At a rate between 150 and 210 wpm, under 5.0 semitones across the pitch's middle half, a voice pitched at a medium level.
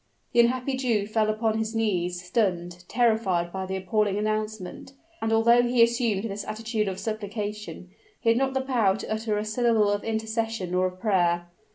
No: average, 180 wpm; average, 3.0 semitones; high, 215 Hz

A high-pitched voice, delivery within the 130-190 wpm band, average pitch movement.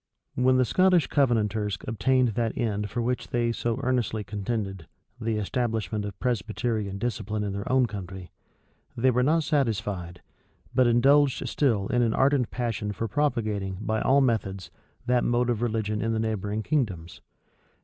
No: low, 115 Hz; average, 155 wpm; average, 3.2 semitones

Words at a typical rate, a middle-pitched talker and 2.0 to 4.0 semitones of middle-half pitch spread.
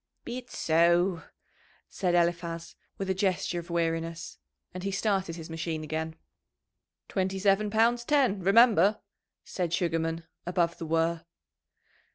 No: slow, 130 wpm; medium, 175 Hz; average, 2.9 semitones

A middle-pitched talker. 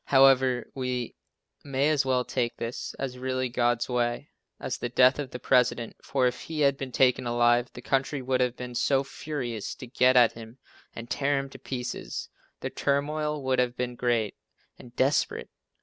No: low, 125 Hz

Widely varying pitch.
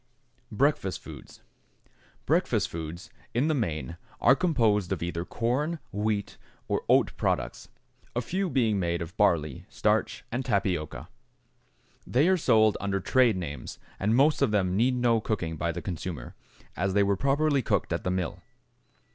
Yes: wide, 6.3 semitones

